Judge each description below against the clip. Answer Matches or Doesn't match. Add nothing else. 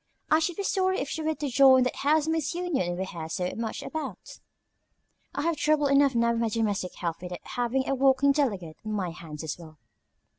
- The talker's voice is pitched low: Doesn't match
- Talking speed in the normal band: Doesn't match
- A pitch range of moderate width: Doesn't match